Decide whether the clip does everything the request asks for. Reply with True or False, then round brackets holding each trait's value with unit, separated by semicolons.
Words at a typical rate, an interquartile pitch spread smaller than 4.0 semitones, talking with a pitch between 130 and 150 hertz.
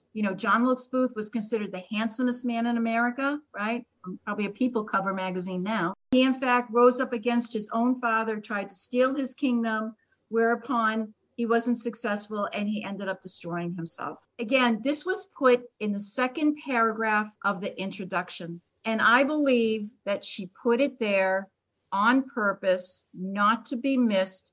False (165 wpm; 3.6 semitones; 225 Hz)